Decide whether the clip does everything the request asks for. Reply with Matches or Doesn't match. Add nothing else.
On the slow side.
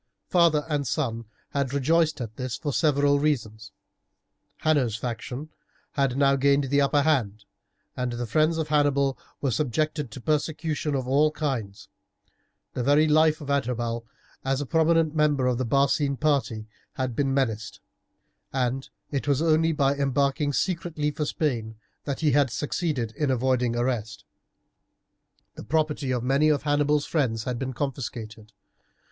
Doesn't match